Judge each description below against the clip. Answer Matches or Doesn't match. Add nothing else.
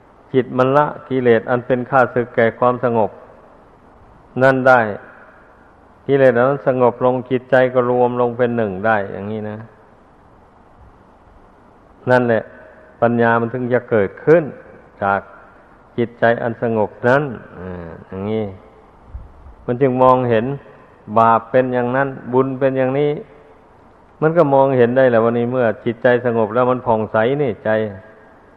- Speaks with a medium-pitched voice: Doesn't match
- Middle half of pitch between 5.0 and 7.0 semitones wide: Doesn't match